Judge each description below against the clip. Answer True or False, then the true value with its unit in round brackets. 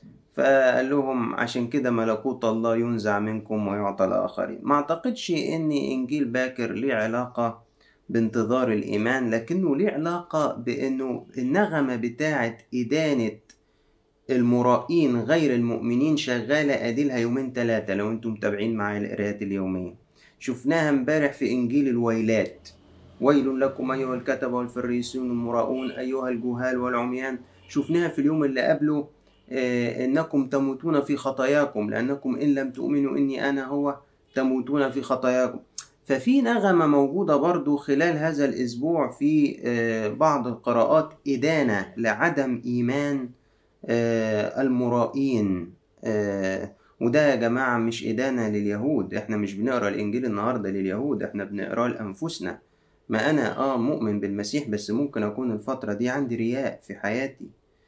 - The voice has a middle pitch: False (125 Hz)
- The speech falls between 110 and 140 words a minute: True (120 wpm)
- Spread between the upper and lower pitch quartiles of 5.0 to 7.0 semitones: False (3.8 semitones)